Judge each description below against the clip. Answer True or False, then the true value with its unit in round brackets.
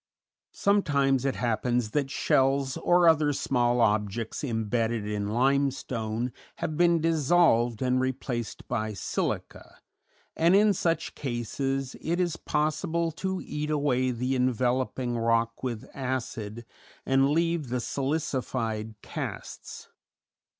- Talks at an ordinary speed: False (115 wpm)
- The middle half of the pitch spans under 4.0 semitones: False (4.3 semitones)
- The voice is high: False (130 Hz)